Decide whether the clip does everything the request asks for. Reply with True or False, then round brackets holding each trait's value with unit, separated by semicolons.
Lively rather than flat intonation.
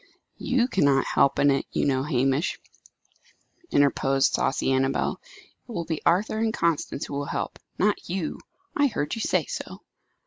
True (6.8 semitones)